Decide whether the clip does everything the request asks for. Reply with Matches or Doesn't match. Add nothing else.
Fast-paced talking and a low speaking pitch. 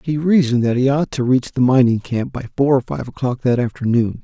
Matches